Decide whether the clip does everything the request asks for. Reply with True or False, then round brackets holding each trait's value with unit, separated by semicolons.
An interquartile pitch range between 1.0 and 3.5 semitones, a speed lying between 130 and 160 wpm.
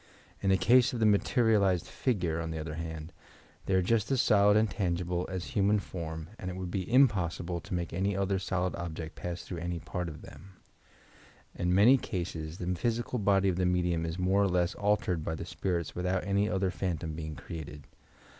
False (2.8 semitones; 200 wpm)